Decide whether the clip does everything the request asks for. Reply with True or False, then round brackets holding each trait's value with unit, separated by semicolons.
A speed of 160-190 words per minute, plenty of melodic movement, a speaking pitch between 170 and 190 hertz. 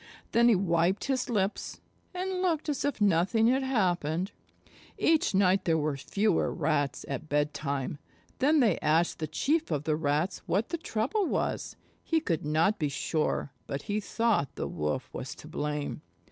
True (165 wpm; 7.7 semitones; 185 Hz)